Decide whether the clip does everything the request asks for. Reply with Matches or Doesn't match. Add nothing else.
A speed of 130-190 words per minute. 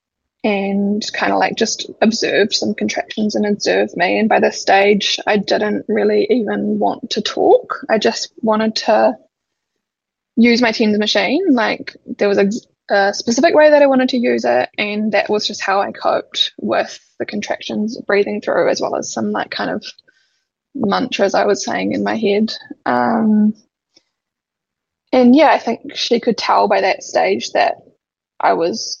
Matches